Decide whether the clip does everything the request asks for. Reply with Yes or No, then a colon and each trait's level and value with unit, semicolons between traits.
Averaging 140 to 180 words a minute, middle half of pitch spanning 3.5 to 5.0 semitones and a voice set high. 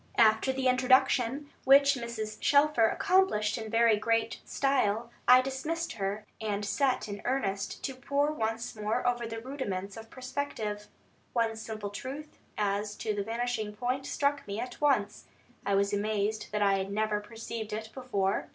Yes: average, 160 wpm; average, 3.8 semitones; high, 225 Hz